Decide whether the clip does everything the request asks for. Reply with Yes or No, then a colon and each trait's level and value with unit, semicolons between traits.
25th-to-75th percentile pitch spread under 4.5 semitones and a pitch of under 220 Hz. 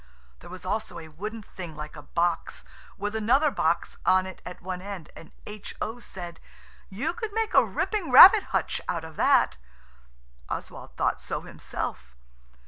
No: average, 5.0 semitones; high, 190 Hz